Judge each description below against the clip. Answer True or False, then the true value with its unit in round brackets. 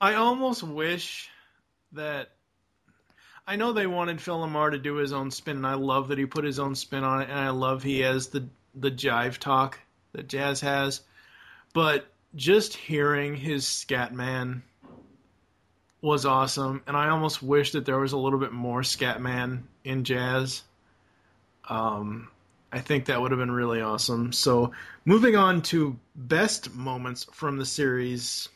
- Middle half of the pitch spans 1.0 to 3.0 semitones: True (2.7 semitones)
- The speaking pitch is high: False (135 Hz)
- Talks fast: False (160 wpm)